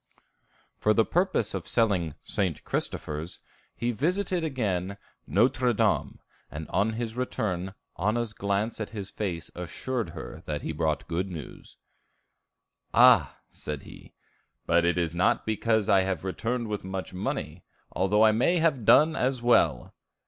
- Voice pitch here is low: Yes, low, 105 Hz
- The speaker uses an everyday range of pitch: Yes, average, 5.0 semitones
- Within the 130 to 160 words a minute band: Yes, average, 145 wpm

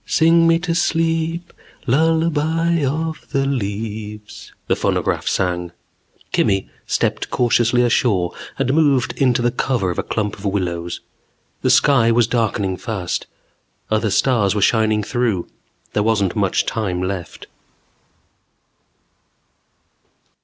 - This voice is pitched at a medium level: No, low, 115 Hz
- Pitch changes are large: Yes, wide, 6.5 semitones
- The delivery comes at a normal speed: No, slow, 115 wpm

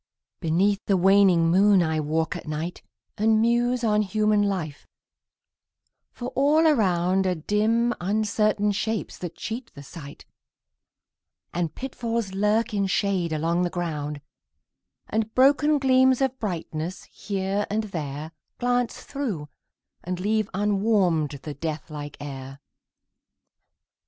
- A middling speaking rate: No, slow, 120 wpm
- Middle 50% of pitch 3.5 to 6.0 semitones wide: Yes, average, 5.1 semitones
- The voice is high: Yes, high, 195 Hz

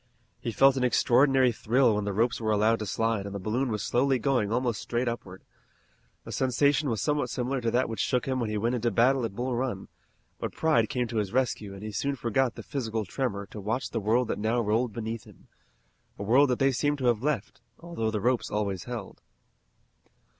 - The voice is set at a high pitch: No, low, 120 Hz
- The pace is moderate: No, fast, 220 wpm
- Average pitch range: Yes, average, 3.3 semitones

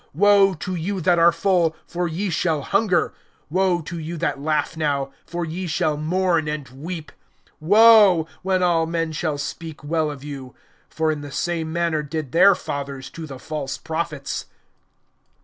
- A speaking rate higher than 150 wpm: Yes, average, 165 wpm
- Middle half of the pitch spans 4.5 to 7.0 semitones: No, average, 2.9 semitones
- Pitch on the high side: No, medium, 165 Hz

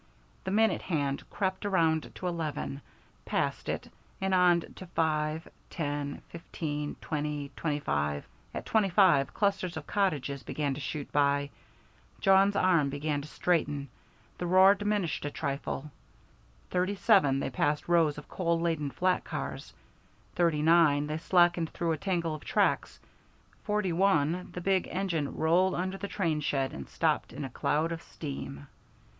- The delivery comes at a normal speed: Yes, average, 150 wpm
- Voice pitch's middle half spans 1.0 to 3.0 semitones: No, average, 4.1 semitones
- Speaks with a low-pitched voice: No, medium, 165 Hz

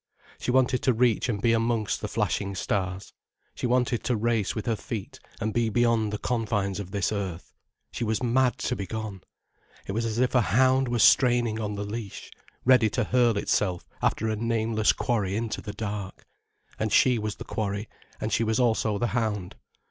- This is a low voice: Yes, low, 110 Hz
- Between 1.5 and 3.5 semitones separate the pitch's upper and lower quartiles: Yes, narrow, 2.6 semitones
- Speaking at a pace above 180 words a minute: Yes, average, 195 wpm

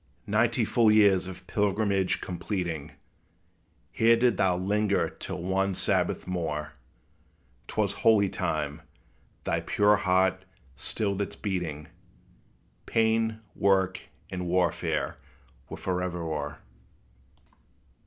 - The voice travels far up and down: No, narrow, 2.6 semitones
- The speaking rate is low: Yes, slow, 105 wpm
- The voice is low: Yes, very low, 95 Hz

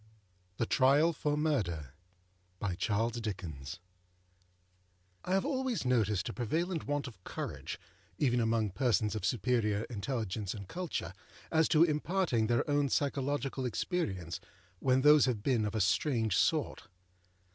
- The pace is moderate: No, slow, 125 wpm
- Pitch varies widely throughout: Yes, wide, 7.4 semitones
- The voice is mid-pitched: No, low, 115 Hz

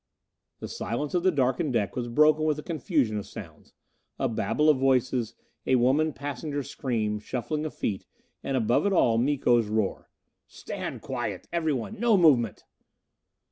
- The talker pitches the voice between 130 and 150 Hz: Yes, low, 135 Hz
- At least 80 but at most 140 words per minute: No, average, 155 wpm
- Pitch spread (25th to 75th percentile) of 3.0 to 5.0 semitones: Yes, average, 4.5 semitones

